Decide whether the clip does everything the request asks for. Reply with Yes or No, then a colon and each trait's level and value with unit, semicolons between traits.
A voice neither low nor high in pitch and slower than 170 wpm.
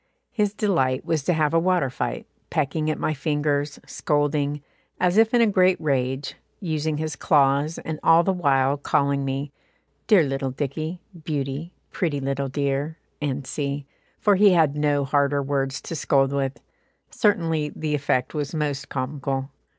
Yes: medium, 145 Hz; average, 155 wpm